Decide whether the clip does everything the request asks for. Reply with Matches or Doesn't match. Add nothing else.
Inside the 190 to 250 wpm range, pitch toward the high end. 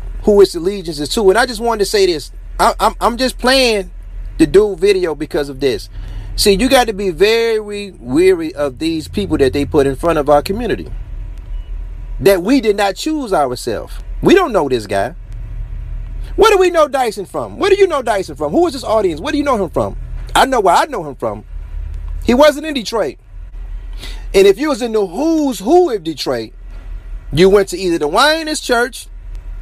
Matches